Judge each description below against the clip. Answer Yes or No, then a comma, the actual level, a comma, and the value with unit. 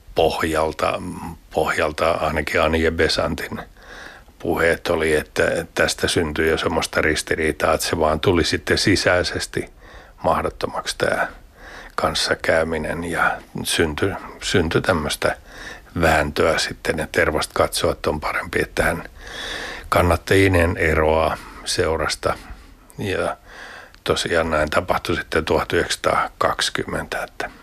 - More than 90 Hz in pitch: No, very low, 80 Hz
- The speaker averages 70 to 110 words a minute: Yes, average, 100 wpm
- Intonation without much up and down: Yes, narrow, 1.4 semitones